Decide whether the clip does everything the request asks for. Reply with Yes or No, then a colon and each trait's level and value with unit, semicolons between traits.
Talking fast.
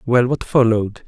No: average, 170 wpm